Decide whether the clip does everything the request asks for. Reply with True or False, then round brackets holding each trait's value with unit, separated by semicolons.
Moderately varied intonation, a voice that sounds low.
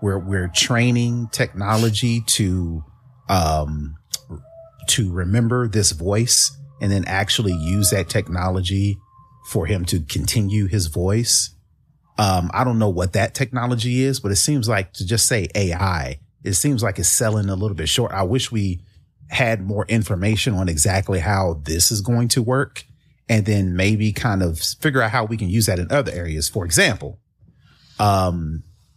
True (4.0 semitones; 105 Hz)